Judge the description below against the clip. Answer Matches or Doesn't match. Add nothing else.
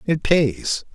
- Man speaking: Matches